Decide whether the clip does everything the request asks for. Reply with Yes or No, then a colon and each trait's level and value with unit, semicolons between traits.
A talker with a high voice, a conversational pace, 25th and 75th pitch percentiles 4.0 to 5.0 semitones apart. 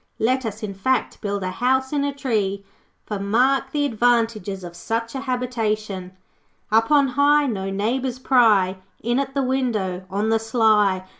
Yes: high, 225 Hz; average, 165 wpm; average, 4.5 semitones